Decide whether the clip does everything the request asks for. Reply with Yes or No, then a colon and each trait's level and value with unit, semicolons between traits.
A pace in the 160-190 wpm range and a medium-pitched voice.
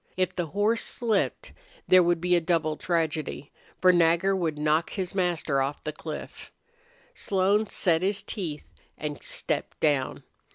No: average, 150 wpm; medium, 175 Hz